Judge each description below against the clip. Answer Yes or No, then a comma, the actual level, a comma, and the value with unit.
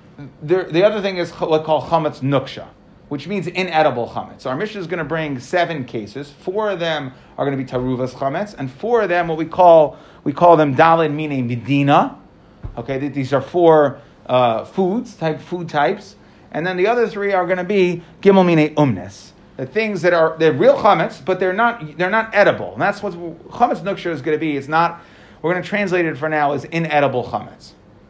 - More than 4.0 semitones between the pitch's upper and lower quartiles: Yes, average, 4.5 semitones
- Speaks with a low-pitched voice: No, medium, 160 Hz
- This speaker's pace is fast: Yes, fast, 215 wpm